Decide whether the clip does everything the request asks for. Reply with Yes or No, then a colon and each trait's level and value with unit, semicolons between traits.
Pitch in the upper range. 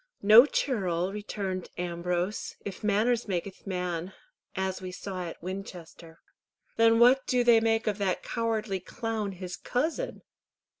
Yes: high, 195 Hz